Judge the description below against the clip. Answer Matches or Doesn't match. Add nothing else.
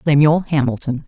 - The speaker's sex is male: Doesn't match